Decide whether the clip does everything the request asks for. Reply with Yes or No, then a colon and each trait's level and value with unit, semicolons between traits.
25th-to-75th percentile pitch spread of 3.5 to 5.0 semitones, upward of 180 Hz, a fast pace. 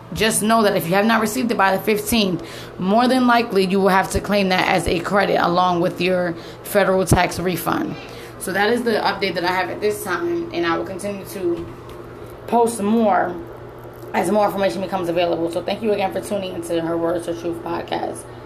No: average, 2.9 semitones; high, 190 Hz; fast, 210 wpm